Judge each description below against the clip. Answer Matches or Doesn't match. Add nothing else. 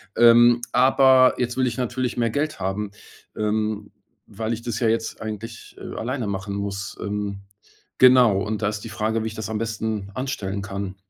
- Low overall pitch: Matches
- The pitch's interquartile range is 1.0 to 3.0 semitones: Matches